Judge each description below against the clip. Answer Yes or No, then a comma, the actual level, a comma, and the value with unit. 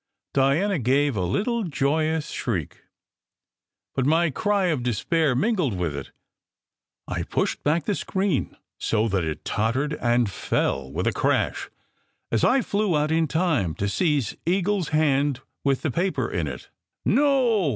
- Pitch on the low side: No, medium, 145 Hz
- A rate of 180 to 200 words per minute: No, average, 155 wpm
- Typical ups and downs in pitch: No, wide, 7.4 semitones